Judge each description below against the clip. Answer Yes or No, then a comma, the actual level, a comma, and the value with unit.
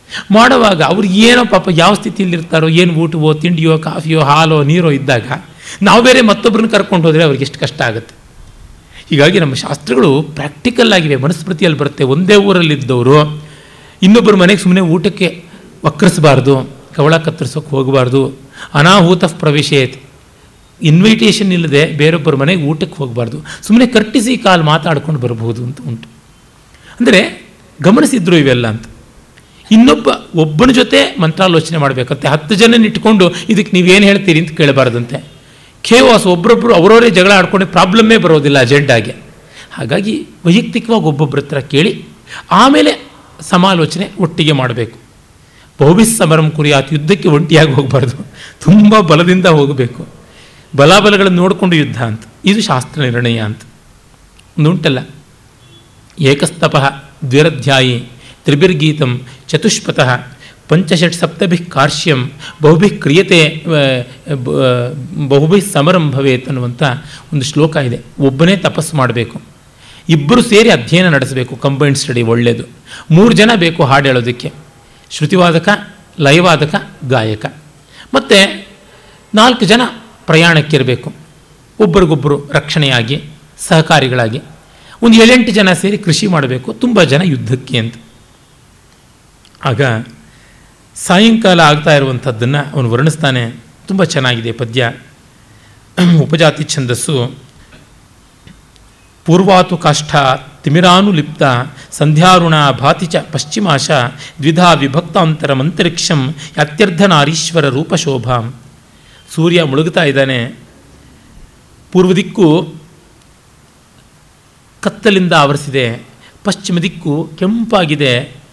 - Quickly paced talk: No, average, 95 wpm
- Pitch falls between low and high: Yes, medium, 155 Hz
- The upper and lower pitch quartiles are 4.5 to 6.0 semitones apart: Yes, average, 5.0 semitones